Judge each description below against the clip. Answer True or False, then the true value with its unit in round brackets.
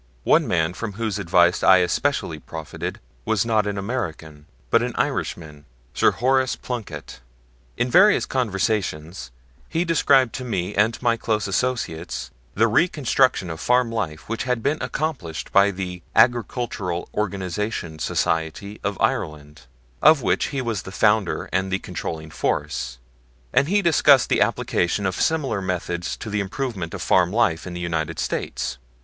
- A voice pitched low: True (100 Hz)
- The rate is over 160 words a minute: False (150 wpm)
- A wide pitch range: True (5.9 semitones)